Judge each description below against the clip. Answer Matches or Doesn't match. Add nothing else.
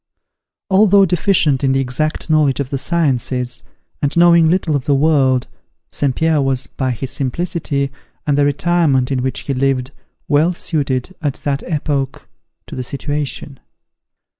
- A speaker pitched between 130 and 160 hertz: Matches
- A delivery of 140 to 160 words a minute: Matches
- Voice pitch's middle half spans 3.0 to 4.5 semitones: Matches